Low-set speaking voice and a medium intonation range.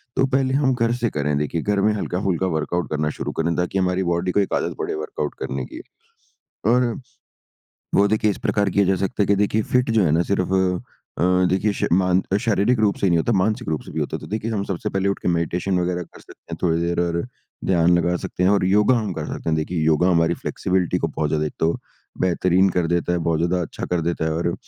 Yes: very low, 90 Hz; average, 3.2 semitones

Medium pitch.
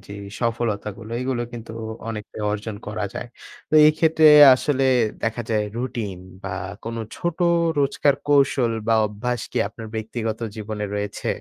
No: low, 115 Hz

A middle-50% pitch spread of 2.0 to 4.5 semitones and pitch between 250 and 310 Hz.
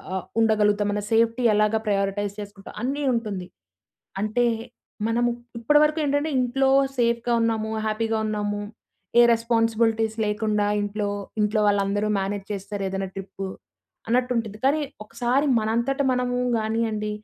No: narrow, 2.5 semitones; high, 220 Hz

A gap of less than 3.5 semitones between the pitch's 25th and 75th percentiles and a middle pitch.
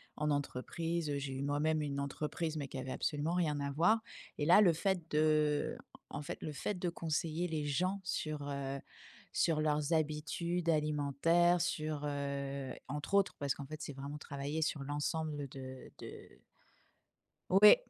Yes: average, 2.7 semitones; medium, 150 Hz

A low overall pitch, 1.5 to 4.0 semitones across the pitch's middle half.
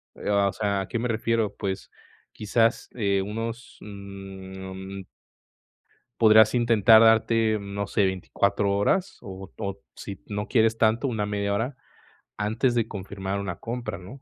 Yes: low, 105 Hz; narrow, 2.4 semitones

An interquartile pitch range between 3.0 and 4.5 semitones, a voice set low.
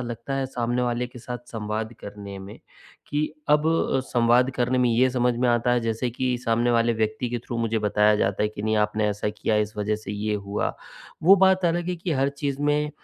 Yes: average, 3.3 semitones; low, 120 Hz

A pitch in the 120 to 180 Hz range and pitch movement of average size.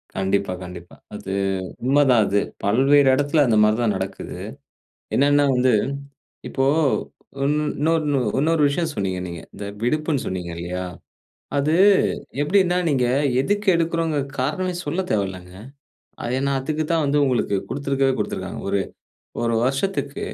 No: low, 135 Hz; wide, 7.0 semitones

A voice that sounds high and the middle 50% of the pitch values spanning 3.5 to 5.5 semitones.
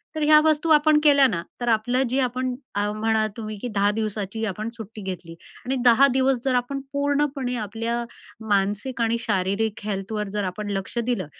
Yes: high, 225 Hz; average, 4.0 semitones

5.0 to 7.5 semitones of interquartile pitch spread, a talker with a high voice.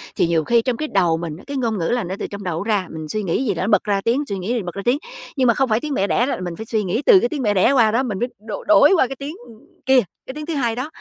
Yes: average, 5.3 semitones; high, 225 Hz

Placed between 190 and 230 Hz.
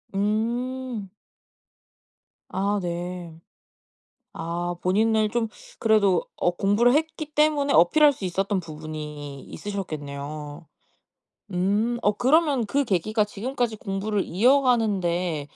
Yes: high, 200 Hz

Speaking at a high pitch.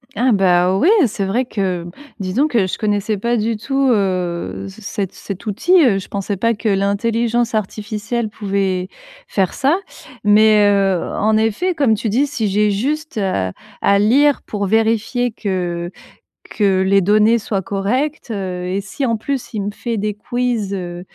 Yes: high, 210 Hz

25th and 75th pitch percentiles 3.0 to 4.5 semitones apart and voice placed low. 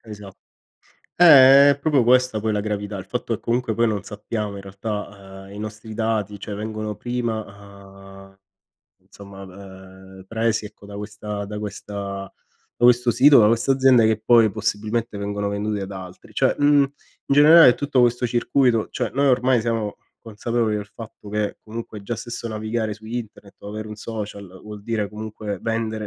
No: narrow, 2.5 semitones; low, 110 Hz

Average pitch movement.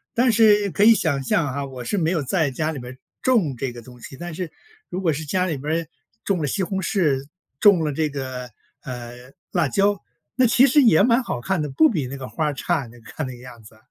No: wide, 6.9 semitones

